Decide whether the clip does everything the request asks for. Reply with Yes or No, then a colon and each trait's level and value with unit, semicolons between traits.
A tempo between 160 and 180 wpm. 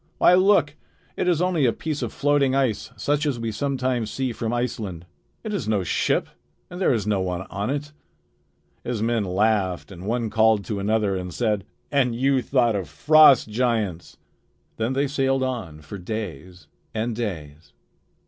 Yes: average, 170 wpm